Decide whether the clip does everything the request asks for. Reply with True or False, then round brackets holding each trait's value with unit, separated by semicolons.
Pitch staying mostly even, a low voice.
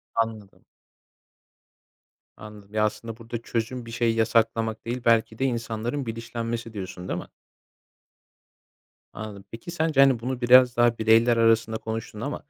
True (1.4 semitones; 115 Hz)